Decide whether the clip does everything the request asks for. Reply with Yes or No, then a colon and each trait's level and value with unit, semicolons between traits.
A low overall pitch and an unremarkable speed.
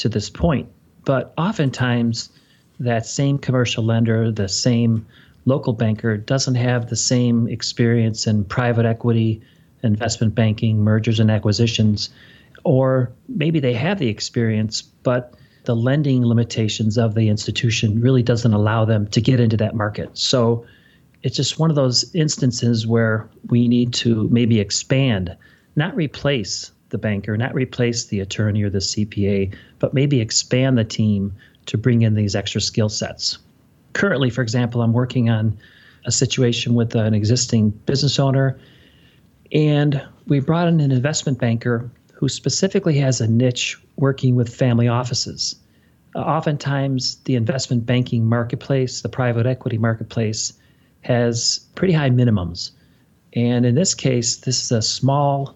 Yes: low, 120 Hz; average, 145 wpm